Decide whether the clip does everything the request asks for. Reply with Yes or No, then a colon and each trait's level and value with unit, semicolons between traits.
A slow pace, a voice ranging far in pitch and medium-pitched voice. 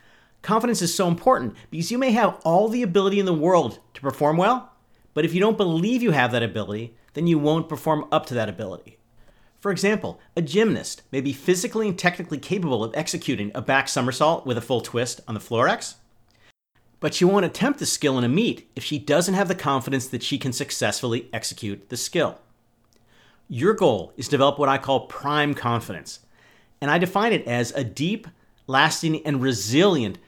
No: average, 195 wpm; wide, 6.8 semitones; medium, 145 Hz